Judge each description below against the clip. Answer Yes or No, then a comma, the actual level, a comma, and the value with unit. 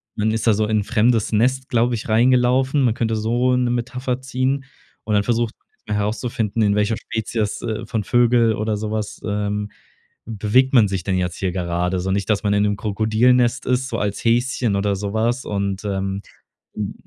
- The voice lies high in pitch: No, low, 110 Hz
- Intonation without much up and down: No, average, 3.0 semitones